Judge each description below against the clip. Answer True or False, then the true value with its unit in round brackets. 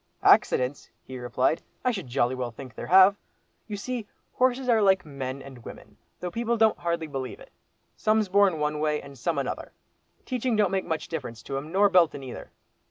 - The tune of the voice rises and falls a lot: True (7.2 semitones)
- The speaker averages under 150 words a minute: False (190 wpm)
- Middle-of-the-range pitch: True (165 Hz)